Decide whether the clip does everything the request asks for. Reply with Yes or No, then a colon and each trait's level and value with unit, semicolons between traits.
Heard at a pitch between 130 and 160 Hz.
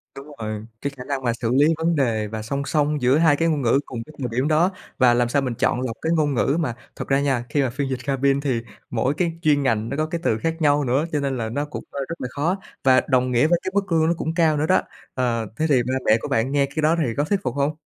Yes: medium, 140 Hz